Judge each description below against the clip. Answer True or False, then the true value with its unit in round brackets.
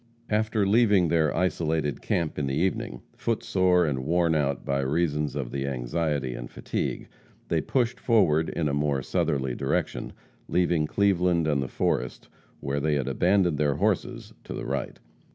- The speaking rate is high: False (165 wpm)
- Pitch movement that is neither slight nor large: True (4.5 semitones)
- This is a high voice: False (75 Hz)